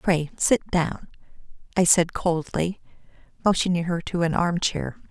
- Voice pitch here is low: No, medium, 170 Hz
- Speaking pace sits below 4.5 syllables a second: Yes, 4.2 syllables/s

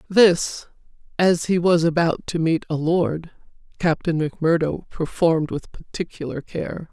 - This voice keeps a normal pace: No, slow, 130 wpm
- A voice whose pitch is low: No, medium, 165 Hz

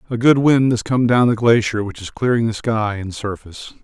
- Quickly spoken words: Yes, fast, 235 wpm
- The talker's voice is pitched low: Yes, low, 115 Hz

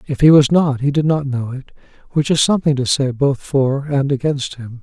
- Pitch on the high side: No, medium, 140 Hz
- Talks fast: Yes, fast, 235 wpm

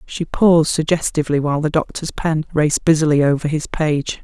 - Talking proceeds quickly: No, average, 170 wpm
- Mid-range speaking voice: Yes, medium, 155 Hz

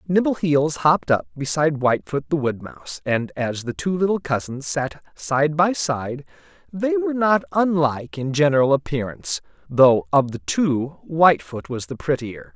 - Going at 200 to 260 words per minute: No, average, 160 wpm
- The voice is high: No, medium, 140 Hz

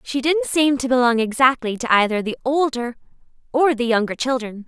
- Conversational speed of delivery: Yes, average, 180 wpm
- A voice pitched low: No, very high, 250 Hz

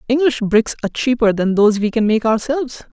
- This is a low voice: No, high, 235 Hz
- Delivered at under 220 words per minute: Yes, average, 200 wpm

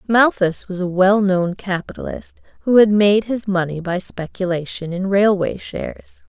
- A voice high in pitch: Yes, high, 195 Hz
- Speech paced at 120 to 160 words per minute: Yes, average, 140 wpm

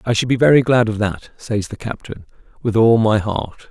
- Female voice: No, male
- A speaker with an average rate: No, fast, 225 wpm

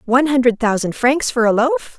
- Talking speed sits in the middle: No, fast, 210 wpm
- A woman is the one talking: Yes, female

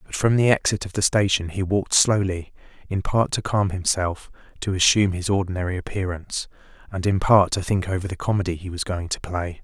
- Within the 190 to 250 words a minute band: Yes, fast, 205 wpm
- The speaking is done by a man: Yes, male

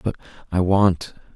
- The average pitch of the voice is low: Yes, very low, 95 Hz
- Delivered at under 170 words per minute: Yes, slow, 135 wpm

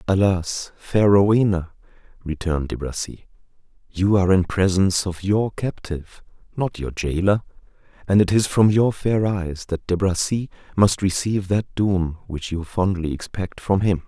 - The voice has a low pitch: Yes, very low, 95 Hz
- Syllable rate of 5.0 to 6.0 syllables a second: No, 4.7 syllables/s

